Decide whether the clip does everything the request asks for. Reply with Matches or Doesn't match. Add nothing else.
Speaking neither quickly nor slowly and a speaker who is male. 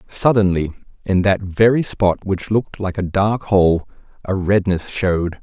Matches